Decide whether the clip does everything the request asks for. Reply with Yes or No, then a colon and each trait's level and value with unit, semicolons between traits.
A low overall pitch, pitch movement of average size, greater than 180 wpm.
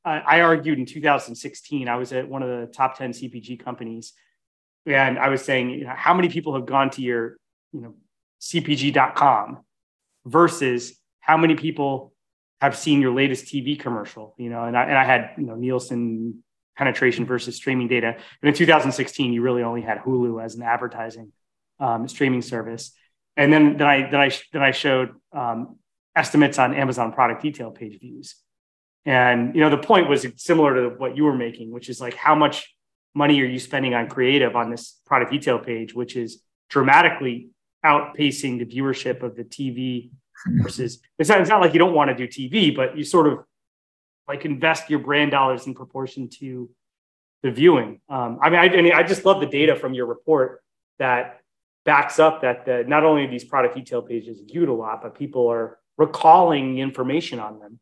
Yes: low, 130 Hz; average, 3.3 semitones; average, 190 wpm